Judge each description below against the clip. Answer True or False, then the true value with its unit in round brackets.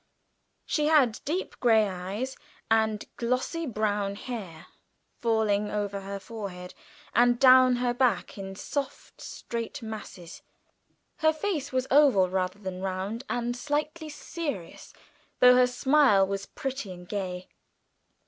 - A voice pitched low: False (225 Hz)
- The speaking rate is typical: False (125 wpm)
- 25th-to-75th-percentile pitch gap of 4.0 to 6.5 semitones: True (4.9 semitones)